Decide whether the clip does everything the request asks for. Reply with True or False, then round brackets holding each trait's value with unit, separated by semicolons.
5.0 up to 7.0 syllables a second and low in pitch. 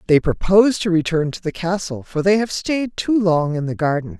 False (5.2 syllables/s; 180 Hz)